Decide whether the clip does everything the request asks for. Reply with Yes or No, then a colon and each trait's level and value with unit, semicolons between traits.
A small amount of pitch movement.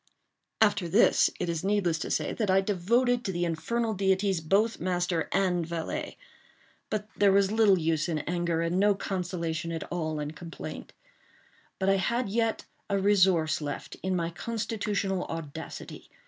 No: average, 3.5 semitones